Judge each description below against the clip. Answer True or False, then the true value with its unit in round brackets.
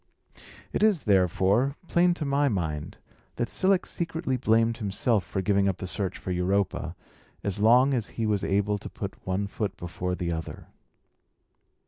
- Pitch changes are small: False (5.4 semitones)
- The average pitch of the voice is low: True (105 Hz)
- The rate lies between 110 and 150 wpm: False (160 wpm)